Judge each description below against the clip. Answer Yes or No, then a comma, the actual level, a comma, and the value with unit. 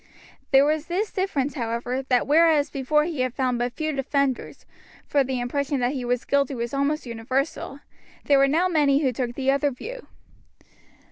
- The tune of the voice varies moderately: Yes, average, 3.0 semitones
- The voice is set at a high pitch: Yes, very high, 275 Hz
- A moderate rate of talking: Yes, average, 180 wpm